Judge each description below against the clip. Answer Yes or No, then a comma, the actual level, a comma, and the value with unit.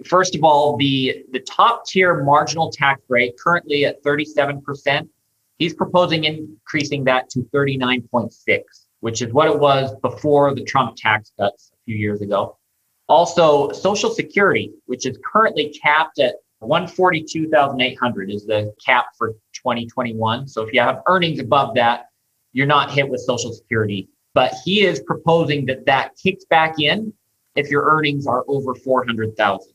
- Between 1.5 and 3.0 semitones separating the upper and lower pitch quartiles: No, average, 4.3 semitones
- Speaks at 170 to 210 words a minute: No, average, 150 wpm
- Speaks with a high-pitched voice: No, medium, 140 Hz